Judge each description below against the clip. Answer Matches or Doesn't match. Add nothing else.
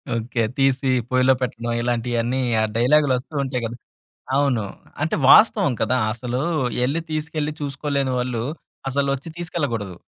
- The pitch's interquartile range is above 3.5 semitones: Doesn't match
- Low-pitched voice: Matches